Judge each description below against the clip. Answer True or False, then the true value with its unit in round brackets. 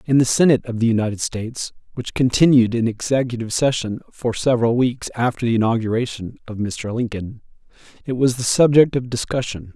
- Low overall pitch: True (120 Hz)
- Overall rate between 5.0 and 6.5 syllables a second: True (5.8 syllables/s)